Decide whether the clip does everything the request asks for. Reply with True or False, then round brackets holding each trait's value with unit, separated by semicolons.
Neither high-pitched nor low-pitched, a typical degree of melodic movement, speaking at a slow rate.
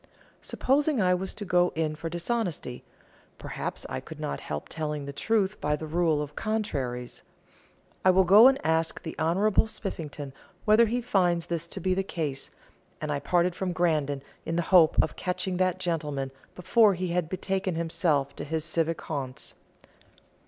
False (170 Hz; 3.8 semitones; 170 wpm)